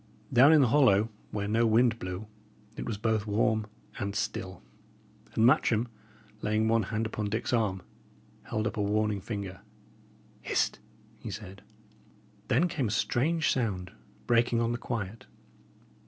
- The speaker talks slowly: No, average, 145 wpm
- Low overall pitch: Yes, low, 110 Hz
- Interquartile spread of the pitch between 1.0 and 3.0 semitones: Yes, narrow, 2.5 semitones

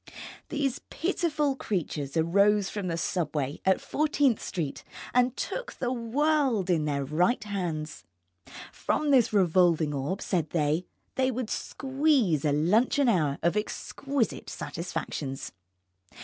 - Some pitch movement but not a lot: No, wide, 8.5 semitones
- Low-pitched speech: No, high, 195 Hz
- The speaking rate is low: Yes, slow, 120 wpm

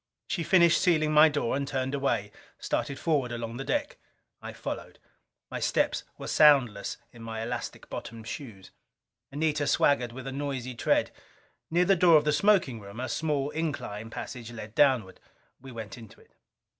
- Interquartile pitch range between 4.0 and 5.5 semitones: Yes, average, 4.7 semitones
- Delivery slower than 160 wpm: No, average, 170 wpm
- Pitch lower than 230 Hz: Yes, low, 135 Hz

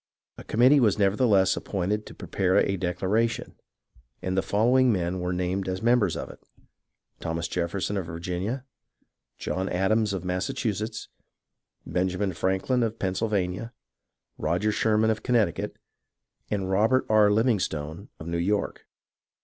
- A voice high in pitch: No, low, 100 Hz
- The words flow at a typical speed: No, slow, 130 wpm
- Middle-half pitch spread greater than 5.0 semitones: No, average, 3.3 semitones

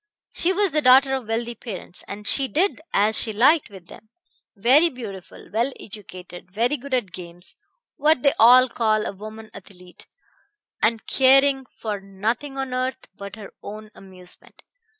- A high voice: Yes, high, 225 Hz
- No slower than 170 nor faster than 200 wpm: No, average, 155 wpm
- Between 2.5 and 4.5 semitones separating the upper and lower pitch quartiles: No, average, 5.0 semitones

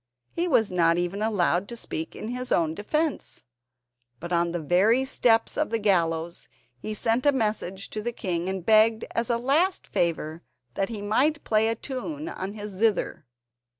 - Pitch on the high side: Yes, high, 215 Hz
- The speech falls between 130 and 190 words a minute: Yes, average, 180 wpm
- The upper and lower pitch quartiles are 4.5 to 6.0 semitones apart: Yes, average, 5.2 semitones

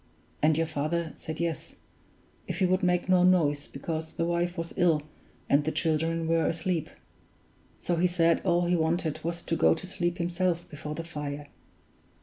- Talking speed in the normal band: Yes, average, 175 wpm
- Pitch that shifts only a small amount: Yes, narrow, 1.8 semitones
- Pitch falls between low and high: Yes, medium, 165 Hz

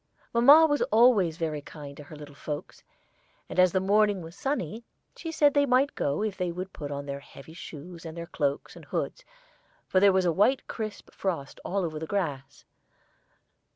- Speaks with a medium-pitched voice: Yes, medium, 180 Hz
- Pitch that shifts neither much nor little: No, wide, 6.0 semitones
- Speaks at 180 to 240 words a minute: Yes, average, 190 wpm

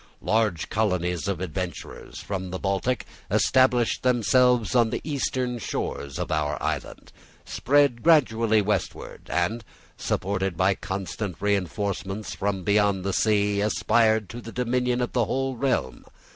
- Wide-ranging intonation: No, average, 4.2 semitones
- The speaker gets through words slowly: Yes, slow, 130 wpm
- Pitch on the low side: Yes, low, 105 Hz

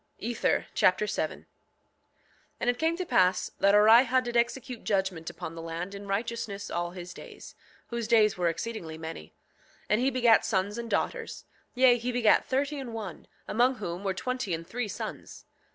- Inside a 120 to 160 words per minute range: No, average, 180 wpm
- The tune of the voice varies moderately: Yes, average, 4.6 semitones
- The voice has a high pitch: Yes, high, 220 Hz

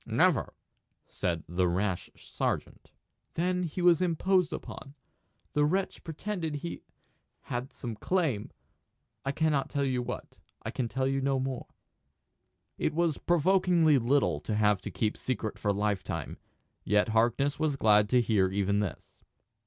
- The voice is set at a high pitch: No, low, 135 Hz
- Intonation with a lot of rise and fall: Yes, wide, 7.3 semitones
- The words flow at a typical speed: Yes, average, 145 wpm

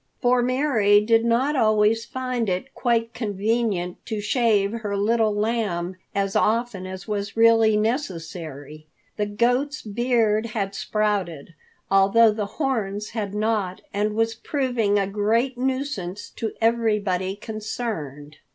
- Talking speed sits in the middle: No, slow, 125 wpm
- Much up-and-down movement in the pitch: No, average, 2.8 semitones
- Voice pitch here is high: Yes, high, 215 Hz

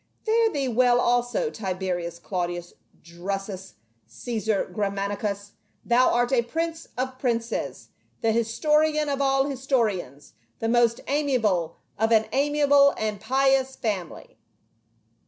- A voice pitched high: Yes, high, 235 Hz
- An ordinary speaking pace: No, slow, 120 wpm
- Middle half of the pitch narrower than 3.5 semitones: No, average, 5.2 semitones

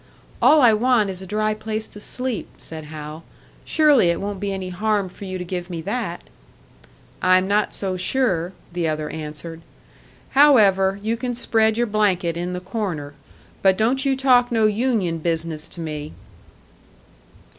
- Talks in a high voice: Yes, high, 195 Hz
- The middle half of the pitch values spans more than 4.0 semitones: Yes, average, 4.5 semitones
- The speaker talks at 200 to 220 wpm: No, average, 165 wpm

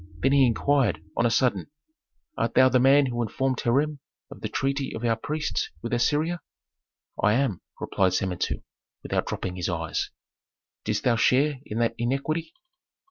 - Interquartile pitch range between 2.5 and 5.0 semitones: Yes, average, 3.7 semitones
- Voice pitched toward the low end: Yes, low, 125 Hz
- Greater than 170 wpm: No, average, 160 wpm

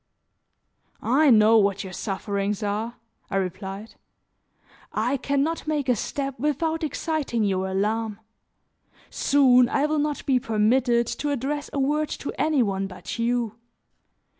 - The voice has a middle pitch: No, high, 240 Hz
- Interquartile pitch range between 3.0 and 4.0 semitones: No, wide, 5.4 semitones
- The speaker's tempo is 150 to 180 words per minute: No, average, 140 wpm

